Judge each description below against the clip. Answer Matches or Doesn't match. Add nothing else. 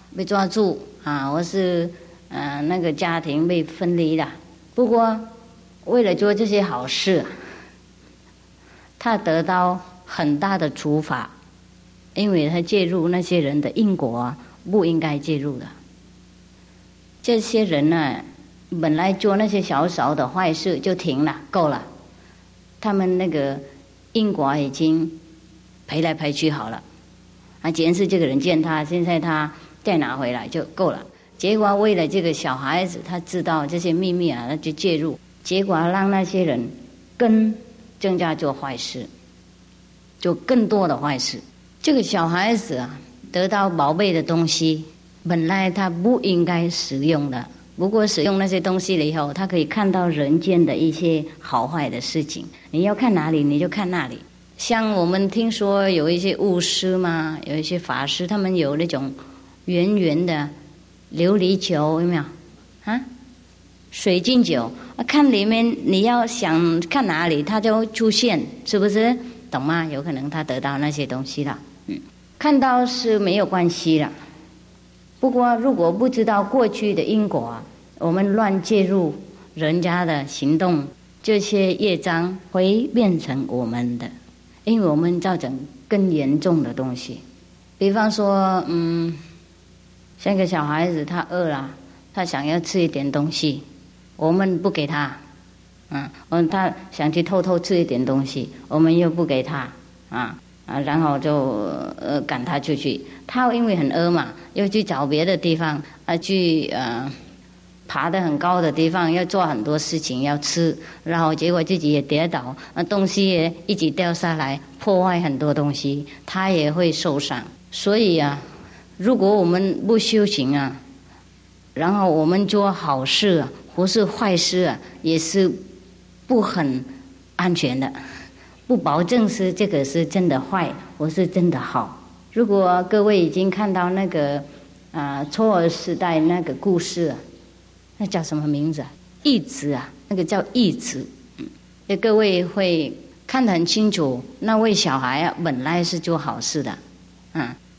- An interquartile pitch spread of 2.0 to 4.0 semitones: Doesn't match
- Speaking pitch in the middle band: Matches